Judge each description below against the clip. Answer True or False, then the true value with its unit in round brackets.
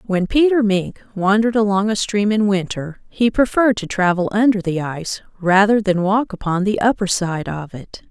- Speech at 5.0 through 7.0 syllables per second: True (5.1 syllables/s)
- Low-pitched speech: False (200 Hz)